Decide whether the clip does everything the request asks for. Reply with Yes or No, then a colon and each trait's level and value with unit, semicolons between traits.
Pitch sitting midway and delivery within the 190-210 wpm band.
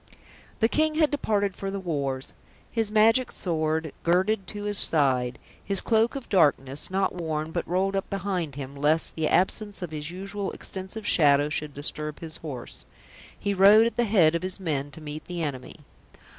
No: medium, 180 Hz; average, 180 wpm